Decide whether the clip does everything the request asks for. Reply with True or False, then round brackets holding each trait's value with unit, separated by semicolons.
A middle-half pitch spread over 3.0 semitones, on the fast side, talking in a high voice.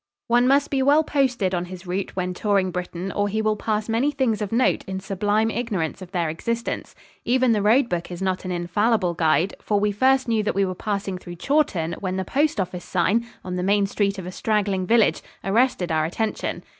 True (4.1 semitones; 210 wpm; 200 Hz)